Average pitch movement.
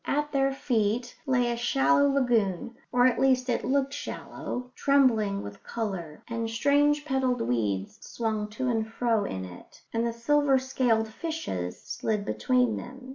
Yes: average, 3.6 semitones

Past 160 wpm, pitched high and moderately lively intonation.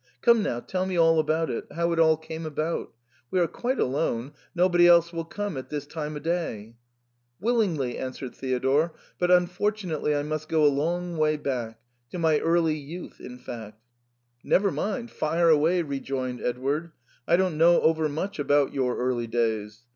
No: average, 185 wpm; medium, 155 Hz; average, 4.6 semitones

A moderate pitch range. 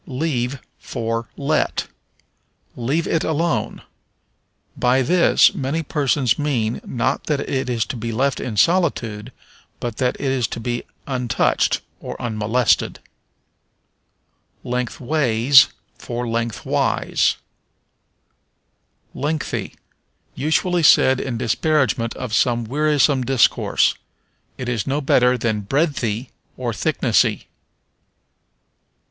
Yes: average, 3.6 semitones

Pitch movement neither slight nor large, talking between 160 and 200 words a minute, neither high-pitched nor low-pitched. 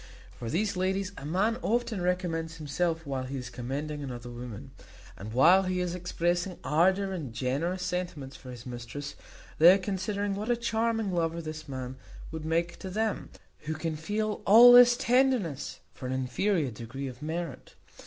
No: wide, 6.0 semitones; average, 170 wpm; medium, 170 Hz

